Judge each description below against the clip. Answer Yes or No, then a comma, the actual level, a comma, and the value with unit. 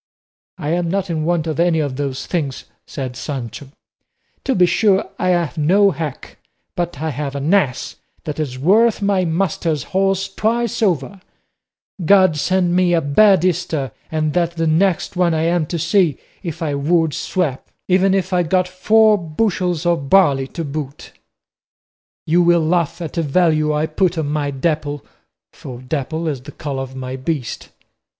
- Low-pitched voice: No, medium, 165 Hz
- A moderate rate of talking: Yes, average, 170 wpm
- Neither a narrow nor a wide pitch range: Yes, average, 3.8 semitones